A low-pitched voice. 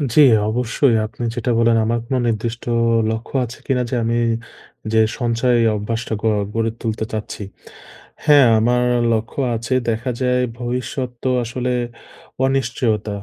Yes: low, 115 Hz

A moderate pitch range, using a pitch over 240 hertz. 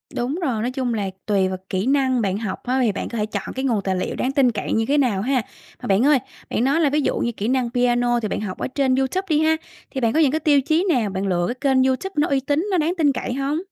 Yes: average, 4.4 semitones; very high, 255 Hz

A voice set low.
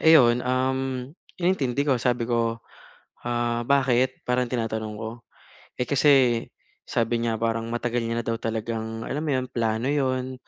Yes: low, 120 Hz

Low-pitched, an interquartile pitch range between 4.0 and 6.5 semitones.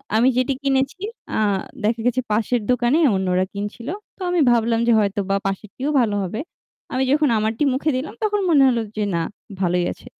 No: high, 235 Hz; average, 4.3 semitones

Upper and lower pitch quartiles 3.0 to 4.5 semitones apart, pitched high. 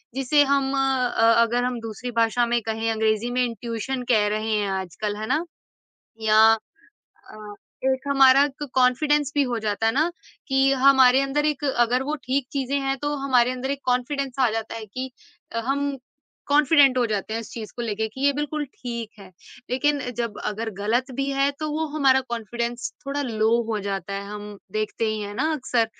Yes: average, 3.7 semitones; very high, 250 Hz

